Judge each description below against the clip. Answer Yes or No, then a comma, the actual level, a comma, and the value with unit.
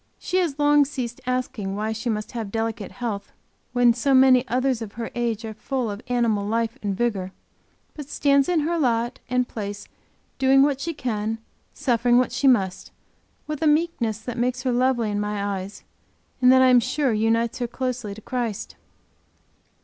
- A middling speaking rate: Yes, average, 180 wpm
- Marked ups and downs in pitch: No, average, 3.2 semitones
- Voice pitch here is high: Yes, high, 240 Hz